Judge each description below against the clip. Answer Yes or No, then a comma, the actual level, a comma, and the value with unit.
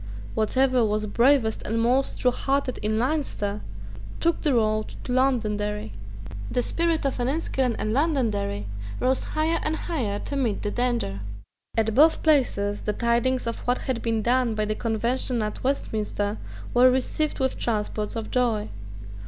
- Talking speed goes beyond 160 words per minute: No, average, 150 wpm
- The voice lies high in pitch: Yes, high, 240 Hz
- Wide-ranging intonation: No, average, 3.7 semitones